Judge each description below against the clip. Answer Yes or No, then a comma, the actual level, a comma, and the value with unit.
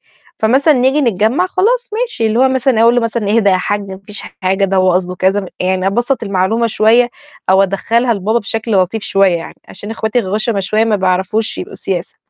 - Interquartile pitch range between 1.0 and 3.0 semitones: No, average, 3.8 semitones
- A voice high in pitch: Yes, high, 215 Hz